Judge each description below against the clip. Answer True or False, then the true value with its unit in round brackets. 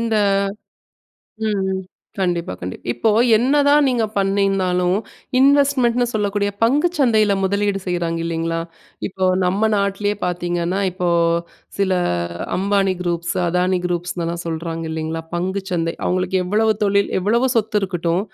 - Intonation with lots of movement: False (3.4 semitones)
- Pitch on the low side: False (190 Hz)